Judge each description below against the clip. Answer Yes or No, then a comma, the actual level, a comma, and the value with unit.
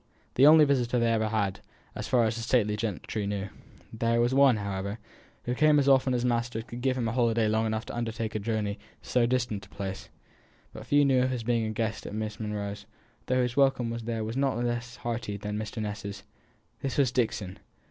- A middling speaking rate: No, fast, 220 wpm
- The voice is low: Yes, low, 115 Hz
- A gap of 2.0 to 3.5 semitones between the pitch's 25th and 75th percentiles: Yes, average, 2.7 semitones